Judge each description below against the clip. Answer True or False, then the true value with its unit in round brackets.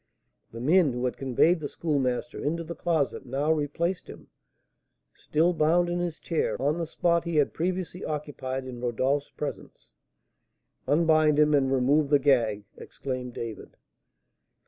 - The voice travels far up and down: False (4.1 semitones)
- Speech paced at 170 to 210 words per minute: False (145 wpm)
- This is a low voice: False (150 Hz)